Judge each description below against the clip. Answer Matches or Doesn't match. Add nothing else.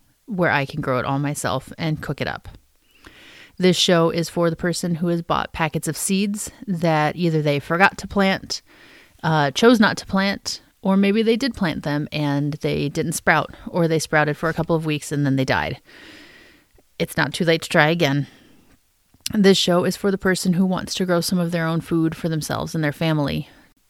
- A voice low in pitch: Doesn't match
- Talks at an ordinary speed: Doesn't match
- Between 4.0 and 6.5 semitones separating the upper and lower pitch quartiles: Doesn't match